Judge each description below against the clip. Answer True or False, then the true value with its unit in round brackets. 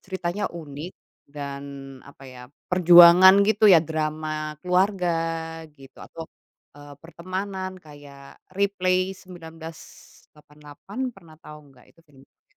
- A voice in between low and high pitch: True (165 Hz)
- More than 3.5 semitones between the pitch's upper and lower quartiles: True (3.9 semitones)